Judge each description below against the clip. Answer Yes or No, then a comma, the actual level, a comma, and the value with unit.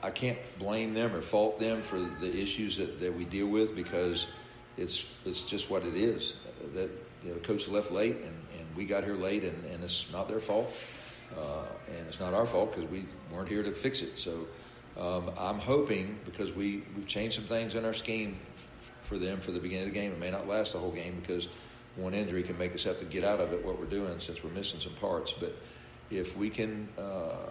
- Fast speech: Yes, fast, 235 wpm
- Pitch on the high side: No, low, 100 Hz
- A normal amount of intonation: Yes, average, 3.1 semitones